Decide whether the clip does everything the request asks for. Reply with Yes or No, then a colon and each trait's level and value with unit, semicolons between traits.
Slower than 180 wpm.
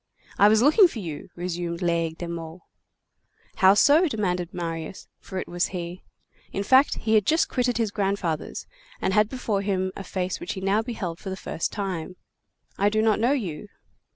No: average, 185 wpm